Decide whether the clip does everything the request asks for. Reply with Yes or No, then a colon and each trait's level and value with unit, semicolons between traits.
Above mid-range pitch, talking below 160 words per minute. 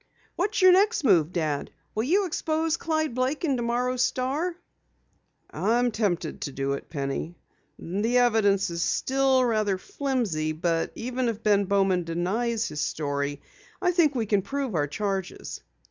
Yes: high, 225 Hz; average, 150 wpm